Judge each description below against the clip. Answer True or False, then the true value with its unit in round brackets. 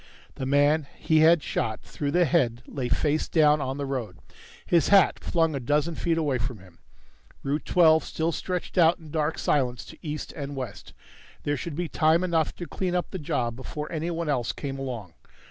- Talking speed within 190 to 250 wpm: True (195 wpm)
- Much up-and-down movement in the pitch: False (3.6 semitones)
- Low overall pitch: False (150 Hz)